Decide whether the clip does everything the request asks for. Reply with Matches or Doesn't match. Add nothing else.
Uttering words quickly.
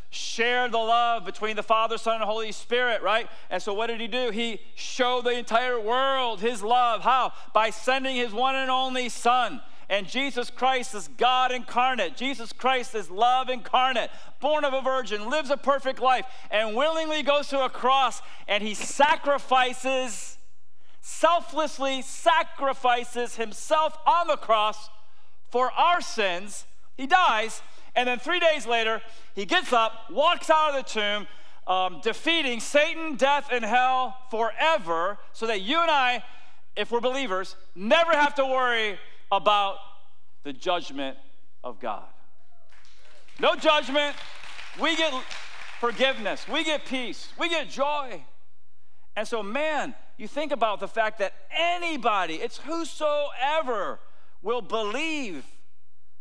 Doesn't match